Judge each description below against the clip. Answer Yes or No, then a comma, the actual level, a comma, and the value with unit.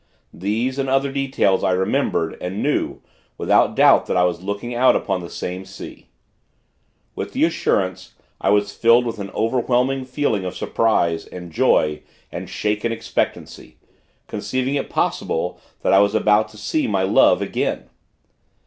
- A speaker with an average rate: Yes, average, 155 wpm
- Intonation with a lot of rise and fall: No, average, 4.9 semitones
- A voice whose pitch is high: No, low, 105 Hz